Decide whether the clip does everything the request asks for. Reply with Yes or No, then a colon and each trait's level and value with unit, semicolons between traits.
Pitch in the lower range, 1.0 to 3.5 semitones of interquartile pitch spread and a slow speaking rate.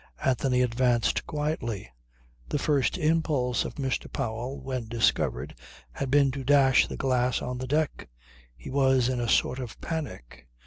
No: low, 130 Hz; narrow, 2.4 semitones; average, 150 wpm